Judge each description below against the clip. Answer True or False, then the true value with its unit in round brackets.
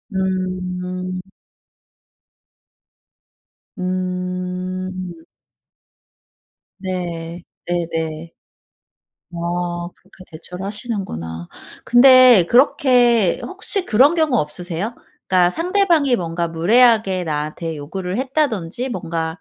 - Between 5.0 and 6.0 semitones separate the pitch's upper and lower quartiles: True (5.4 semitones)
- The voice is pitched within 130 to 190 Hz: True (185 Hz)